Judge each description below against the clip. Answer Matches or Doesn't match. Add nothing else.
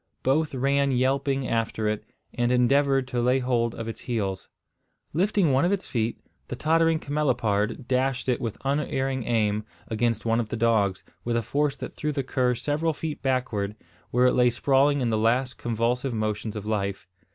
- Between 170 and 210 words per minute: Matches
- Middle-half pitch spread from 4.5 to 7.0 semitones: Doesn't match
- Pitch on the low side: Matches